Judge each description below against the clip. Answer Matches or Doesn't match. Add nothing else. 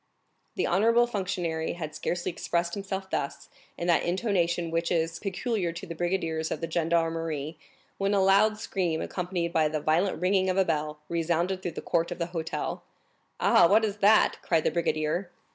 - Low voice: Doesn't match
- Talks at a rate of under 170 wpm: Doesn't match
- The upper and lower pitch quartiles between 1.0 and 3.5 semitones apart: Matches